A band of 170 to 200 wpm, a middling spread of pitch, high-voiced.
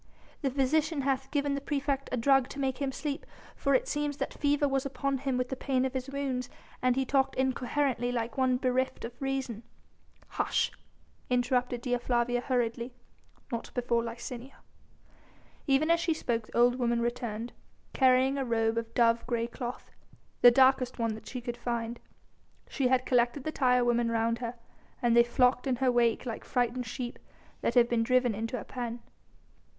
No: average, 180 wpm; narrow, 2.2 semitones; very high, 250 Hz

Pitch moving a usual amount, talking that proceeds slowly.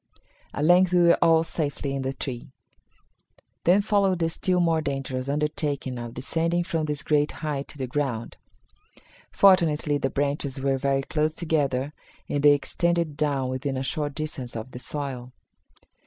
No: average, 3.3 semitones; average, 160 wpm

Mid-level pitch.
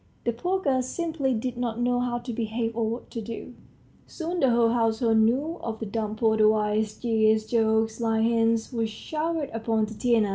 No: high, 230 Hz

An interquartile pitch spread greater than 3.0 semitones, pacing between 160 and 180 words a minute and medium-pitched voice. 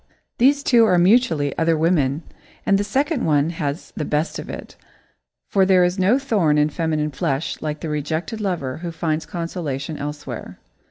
Yes: average, 4.4 semitones; average, 170 wpm; medium, 165 Hz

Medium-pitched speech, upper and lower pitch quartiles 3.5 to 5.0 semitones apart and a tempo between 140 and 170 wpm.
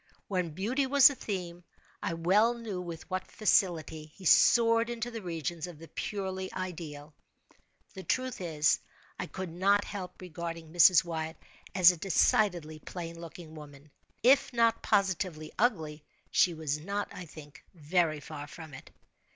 Yes: medium, 175 Hz; average, 4.0 semitones; average, 150 wpm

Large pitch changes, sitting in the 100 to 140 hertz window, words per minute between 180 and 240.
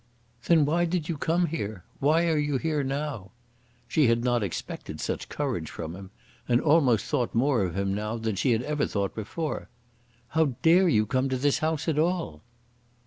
Yes: wide, 6.1 semitones; low, 135 Hz; average, 190 wpm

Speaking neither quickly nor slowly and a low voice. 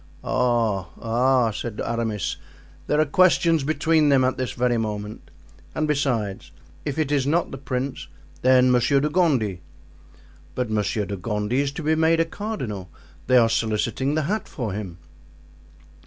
Yes: average, 155 wpm; low, 125 Hz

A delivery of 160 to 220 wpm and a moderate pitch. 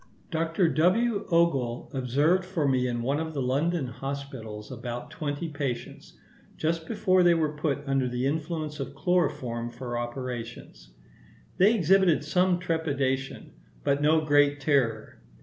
No: slow, 135 wpm; medium, 145 Hz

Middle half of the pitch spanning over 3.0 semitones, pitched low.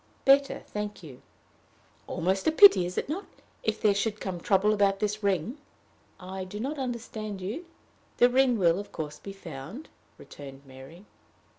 No: average, 4.6 semitones; high, 200 Hz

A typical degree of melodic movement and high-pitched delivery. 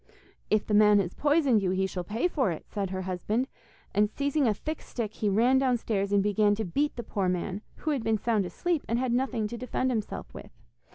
Yes: average, 4.3 semitones; high, 215 Hz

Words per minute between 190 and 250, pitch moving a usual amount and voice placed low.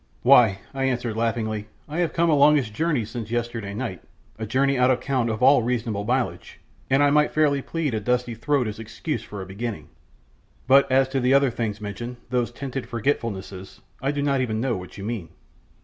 Yes: average, 200 wpm; average, 3.9 semitones; low, 120 Hz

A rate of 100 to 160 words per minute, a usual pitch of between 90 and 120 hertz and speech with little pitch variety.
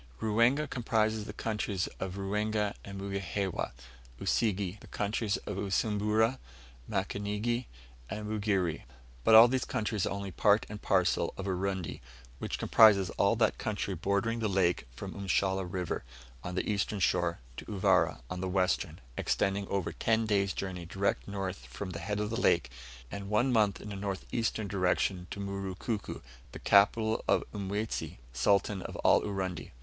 Yes: average, 155 wpm; low, 100 Hz; narrow, 2.1 semitones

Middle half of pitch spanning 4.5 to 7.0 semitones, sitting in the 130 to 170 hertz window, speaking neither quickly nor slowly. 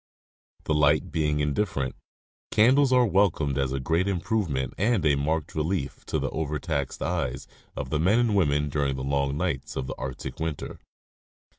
No: average, 4.9 semitones; very low, 75 Hz; average, 170 wpm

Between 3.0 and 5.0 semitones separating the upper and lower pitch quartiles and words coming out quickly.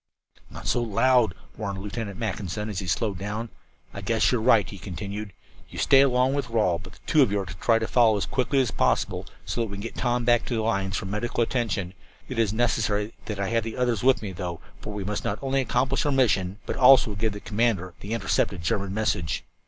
Yes: average, 3.4 semitones; fast, 230 wpm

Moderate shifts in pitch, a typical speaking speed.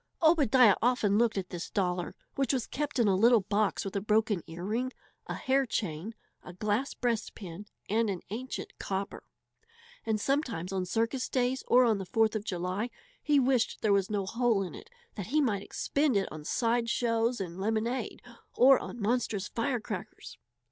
Yes: average, 4.0 semitones; average, 175 wpm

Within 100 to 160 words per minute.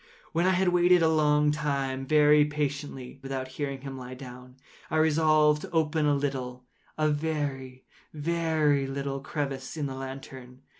Yes: average, 150 wpm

